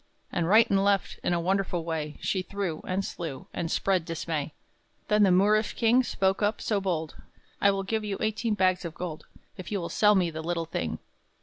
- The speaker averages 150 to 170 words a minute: No, fast, 205 wpm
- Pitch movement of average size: Yes, average, 3.3 semitones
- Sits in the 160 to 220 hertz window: Yes, high, 190 Hz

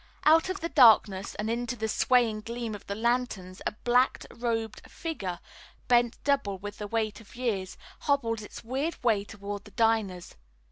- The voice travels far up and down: No, average, 3.2 semitones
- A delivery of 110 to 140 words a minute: No, average, 170 wpm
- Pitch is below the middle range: No, high, 225 Hz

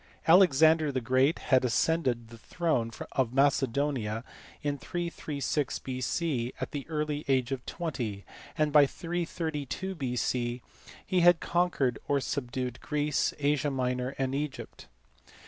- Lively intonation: No, average, 3.7 semitones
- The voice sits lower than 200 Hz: Yes, medium, 140 Hz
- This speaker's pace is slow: Yes, slow, 130 wpm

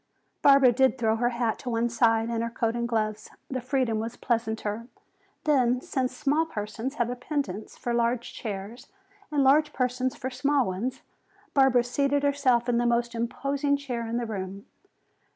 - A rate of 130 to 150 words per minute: No, average, 170 wpm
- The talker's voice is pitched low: No, high, 240 Hz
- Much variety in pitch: No, average, 2.7 semitones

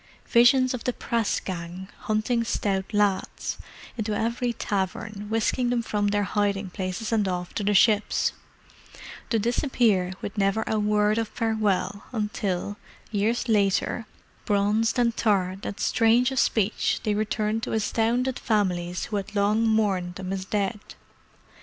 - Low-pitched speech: No, high, 210 Hz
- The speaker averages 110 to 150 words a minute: Yes, average, 145 wpm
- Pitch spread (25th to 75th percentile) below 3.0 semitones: Yes, narrow, 2.4 semitones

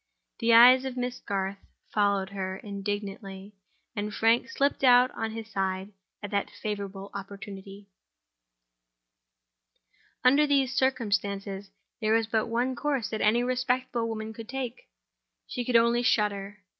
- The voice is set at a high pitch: Yes, high, 220 Hz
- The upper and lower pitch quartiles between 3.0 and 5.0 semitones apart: Yes, average, 3.6 semitones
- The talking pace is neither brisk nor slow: No, slow, 130 wpm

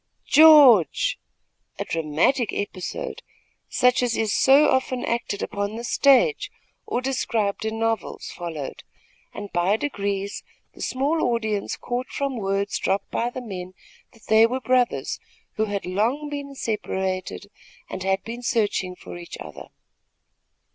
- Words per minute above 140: No, slow, 135 wpm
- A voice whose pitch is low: No, high, 225 Hz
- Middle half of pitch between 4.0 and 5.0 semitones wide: Yes, average, 4.6 semitones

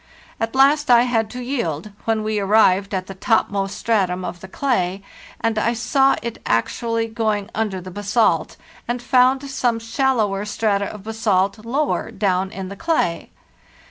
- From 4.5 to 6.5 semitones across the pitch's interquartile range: No, average, 3.6 semitones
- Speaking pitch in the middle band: No, high, 220 Hz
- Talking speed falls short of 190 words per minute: Yes, average, 160 wpm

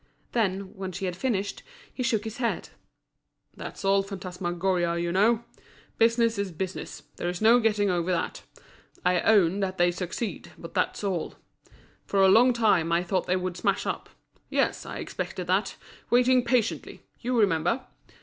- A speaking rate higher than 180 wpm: No, average, 155 wpm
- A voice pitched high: Yes, high, 195 Hz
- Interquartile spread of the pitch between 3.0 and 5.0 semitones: Yes, average, 4.0 semitones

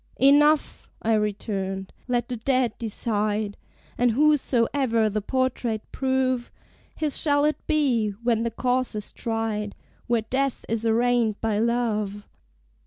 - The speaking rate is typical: No, slow, 125 wpm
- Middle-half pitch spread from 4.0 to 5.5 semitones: No, average, 3.2 semitones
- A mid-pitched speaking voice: No, high, 235 Hz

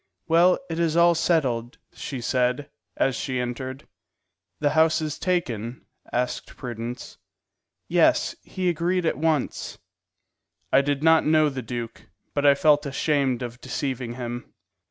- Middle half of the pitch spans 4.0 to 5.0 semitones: Yes, average, 4.5 semitones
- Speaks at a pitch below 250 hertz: Yes, medium, 140 Hz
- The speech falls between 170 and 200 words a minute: No, slow, 135 wpm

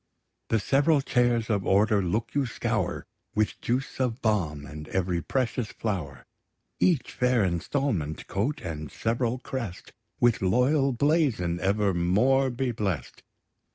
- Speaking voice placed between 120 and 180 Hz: No, low, 110 Hz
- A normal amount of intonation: No, wide, 5.9 semitones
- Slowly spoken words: Yes, slow, 125 wpm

